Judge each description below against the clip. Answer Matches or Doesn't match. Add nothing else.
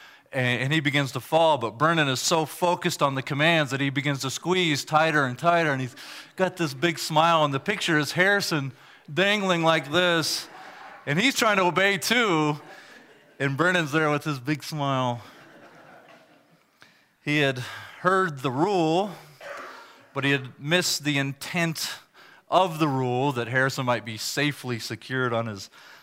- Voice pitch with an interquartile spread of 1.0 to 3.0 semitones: Doesn't match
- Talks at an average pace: Matches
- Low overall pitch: Doesn't match